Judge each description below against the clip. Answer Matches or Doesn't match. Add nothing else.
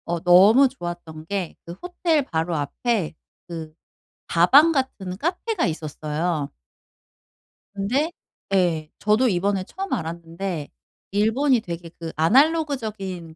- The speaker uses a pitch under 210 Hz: Matches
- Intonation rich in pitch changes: Matches